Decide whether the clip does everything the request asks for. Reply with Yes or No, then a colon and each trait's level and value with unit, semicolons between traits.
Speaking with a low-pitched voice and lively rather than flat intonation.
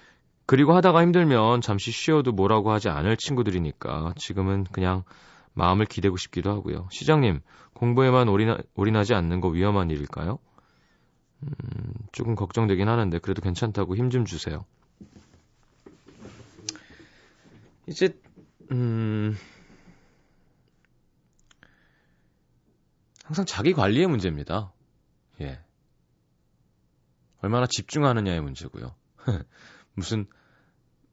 No: low, 105 Hz; average, 4.9 semitones